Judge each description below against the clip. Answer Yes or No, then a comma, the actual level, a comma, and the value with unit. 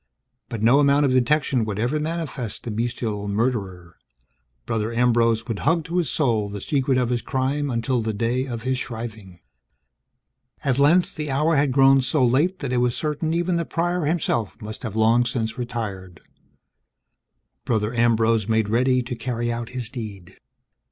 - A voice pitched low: Yes, low, 120 Hz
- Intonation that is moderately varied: Yes, average, 3.8 semitones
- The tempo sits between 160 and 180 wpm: Yes, average, 170 wpm